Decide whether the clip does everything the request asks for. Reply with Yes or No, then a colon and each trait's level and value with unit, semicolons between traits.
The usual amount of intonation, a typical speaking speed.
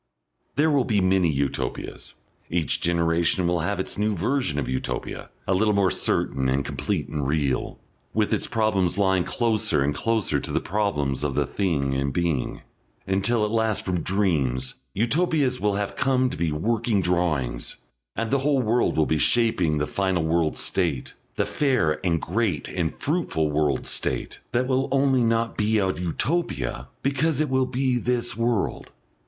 No: wide, 6.9 semitones; average, 170 wpm